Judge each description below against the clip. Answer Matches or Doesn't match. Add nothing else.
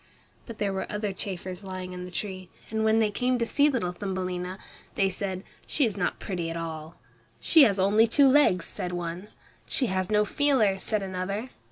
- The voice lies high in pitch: Matches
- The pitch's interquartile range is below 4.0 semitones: Matches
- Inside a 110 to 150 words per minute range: Doesn't match